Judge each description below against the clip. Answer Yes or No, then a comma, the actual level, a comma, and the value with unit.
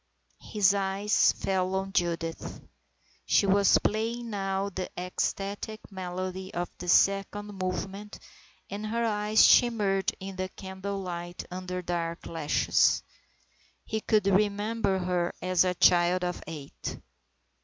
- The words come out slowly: Yes, slow, 125 wpm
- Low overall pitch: No, high, 190 Hz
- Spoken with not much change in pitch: Yes, narrow, 2.1 semitones